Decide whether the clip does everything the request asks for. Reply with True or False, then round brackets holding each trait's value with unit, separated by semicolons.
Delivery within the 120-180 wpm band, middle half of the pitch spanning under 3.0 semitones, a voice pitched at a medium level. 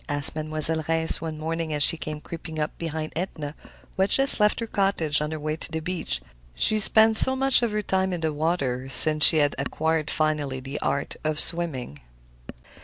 False (195 wpm; 2.5 semitones; 155 Hz)